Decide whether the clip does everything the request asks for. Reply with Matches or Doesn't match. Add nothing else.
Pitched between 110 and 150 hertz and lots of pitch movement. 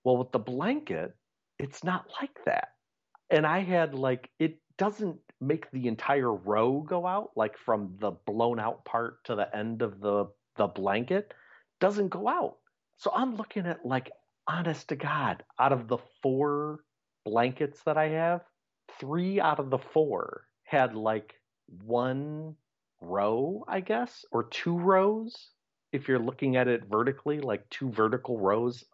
Matches